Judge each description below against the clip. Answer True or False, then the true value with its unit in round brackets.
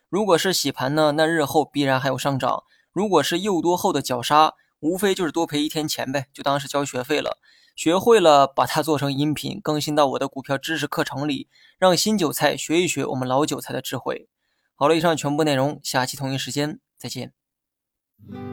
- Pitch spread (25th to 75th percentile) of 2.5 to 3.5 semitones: True (2.9 semitones)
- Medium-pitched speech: True (150 Hz)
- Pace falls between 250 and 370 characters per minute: True (300 characters per minute)